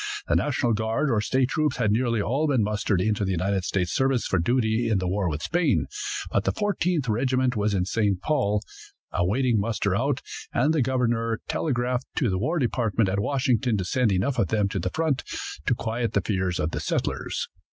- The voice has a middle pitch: No, low, 115 Hz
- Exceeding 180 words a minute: Yes, average, 200 wpm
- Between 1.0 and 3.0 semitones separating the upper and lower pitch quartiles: No, average, 4.6 semitones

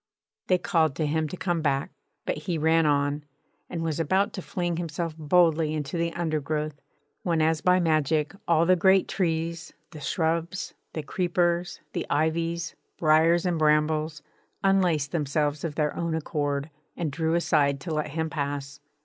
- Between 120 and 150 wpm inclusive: No, average, 160 wpm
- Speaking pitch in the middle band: Yes, medium, 160 Hz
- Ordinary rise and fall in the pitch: No, narrow, 2.1 semitones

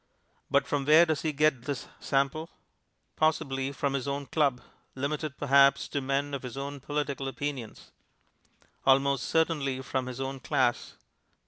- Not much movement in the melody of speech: Yes, narrow, 1.4 semitones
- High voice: No, medium, 140 Hz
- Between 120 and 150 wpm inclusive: Yes, average, 145 wpm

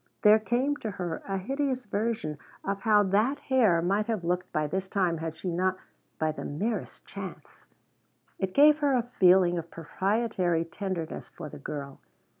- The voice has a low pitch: No, high, 190 Hz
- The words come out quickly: No, average, 170 wpm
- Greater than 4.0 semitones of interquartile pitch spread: Yes, average, 5.0 semitones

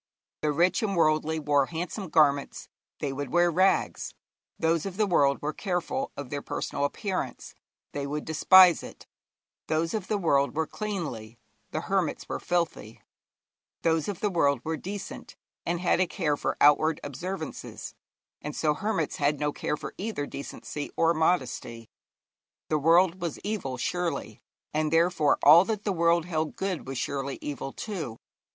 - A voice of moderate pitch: Yes, medium, 160 Hz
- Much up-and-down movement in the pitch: No, average, 3.8 semitones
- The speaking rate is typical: Yes, average, 160 wpm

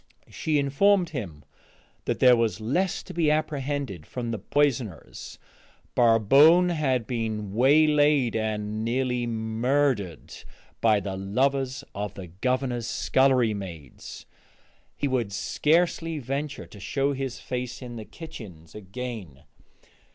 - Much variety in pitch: No, average, 4.9 semitones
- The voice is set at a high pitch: No, low, 125 Hz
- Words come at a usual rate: No, slow, 120 wpm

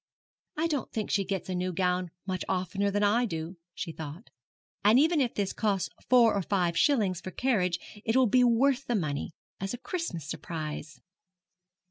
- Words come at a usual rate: Yes, average, 180 wpm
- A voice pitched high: Yes, high, 195 Hz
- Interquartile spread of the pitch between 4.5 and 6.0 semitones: Yes, average, 5.2 semitones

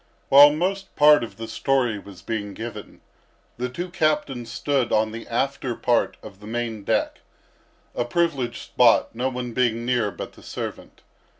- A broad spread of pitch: No, average, 3.5 semitones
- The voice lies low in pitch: Yes, low, 120 Hz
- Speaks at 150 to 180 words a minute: Yes, average, 165 wpm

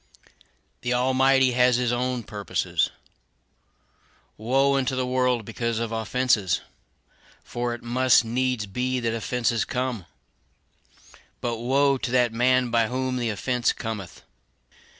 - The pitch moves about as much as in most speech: No, narrow, 1.8 semitones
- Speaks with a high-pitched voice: No, low, 125 Hz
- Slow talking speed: Yes, slow, 125 wpm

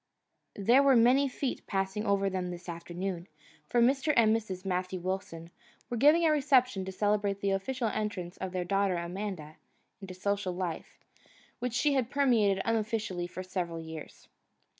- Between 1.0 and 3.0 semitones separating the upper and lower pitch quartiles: No, average, 4.5 semitones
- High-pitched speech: Yes, high, 195 Hz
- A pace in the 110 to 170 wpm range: Yes, average, 160 wpm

